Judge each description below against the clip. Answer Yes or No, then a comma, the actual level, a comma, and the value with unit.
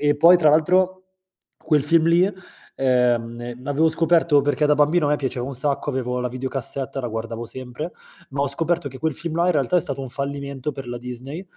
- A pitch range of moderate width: Yes, average, 3.7 semitones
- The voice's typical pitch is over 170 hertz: No, medium, 145 Hz